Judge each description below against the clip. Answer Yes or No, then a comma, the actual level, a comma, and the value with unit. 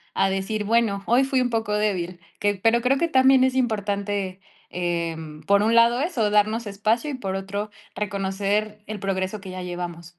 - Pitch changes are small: No, average, 3.3 semitones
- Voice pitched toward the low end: No, high, 205 Hz